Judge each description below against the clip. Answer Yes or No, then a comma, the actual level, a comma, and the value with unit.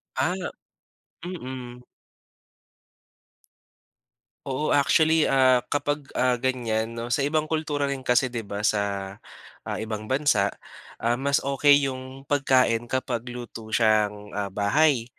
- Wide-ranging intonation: No, average, 4.0 semitones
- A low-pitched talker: Yes, low, 125 Hz